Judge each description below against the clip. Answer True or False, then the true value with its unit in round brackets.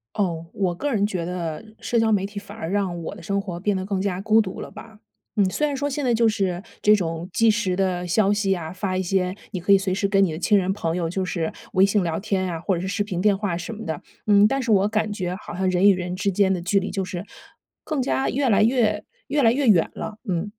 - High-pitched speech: True (195 Hz)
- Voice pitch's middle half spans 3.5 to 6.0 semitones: False (2.8 semitones)